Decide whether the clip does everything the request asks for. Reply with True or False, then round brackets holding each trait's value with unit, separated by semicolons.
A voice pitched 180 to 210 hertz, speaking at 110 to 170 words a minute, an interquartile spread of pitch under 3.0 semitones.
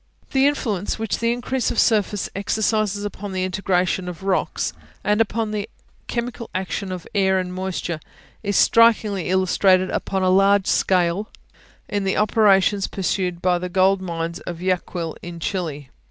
True (190 Hz; 155 wpm; 2.4 semitones)